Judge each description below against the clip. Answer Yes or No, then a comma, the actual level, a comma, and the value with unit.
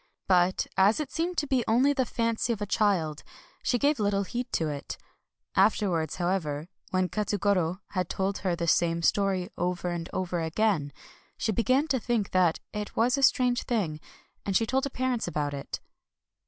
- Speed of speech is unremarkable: Yes, average, 180 wpm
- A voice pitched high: Yes, high, 200 Hz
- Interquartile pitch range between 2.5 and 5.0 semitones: No, wide, 5.4 semitones